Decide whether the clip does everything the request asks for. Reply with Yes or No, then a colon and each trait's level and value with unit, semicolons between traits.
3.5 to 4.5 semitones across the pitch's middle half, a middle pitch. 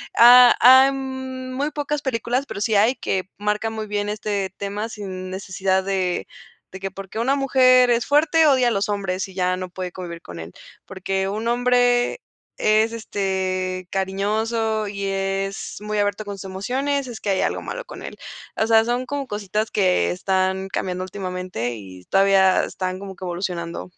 No: average, 4.2 semitones; high, 205 Hz